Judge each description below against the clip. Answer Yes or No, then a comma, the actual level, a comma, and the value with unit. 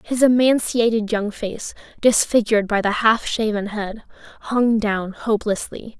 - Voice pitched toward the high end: Yes, high, 220 Hz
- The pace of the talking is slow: Yes, slow, 130 wpm